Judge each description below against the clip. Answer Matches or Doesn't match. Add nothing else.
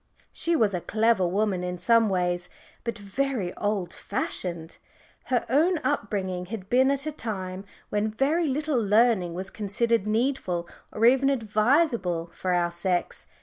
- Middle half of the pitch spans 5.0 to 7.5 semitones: Matches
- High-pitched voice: Matches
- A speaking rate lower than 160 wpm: Matches